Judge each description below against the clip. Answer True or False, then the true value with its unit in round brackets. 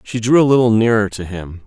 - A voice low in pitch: True (110 Hz)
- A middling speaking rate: False (255 wpm)